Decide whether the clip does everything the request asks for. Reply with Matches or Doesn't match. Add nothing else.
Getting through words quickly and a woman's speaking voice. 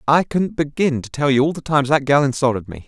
Doesn't match